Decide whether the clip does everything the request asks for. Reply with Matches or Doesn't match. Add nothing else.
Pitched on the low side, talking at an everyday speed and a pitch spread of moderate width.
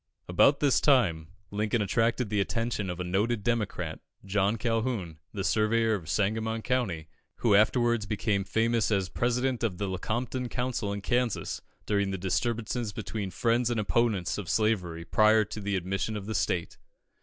Matches